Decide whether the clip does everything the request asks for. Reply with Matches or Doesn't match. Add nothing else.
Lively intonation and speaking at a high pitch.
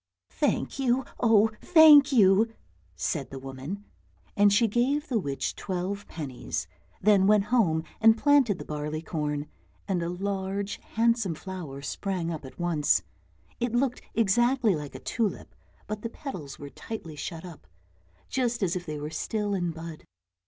Matches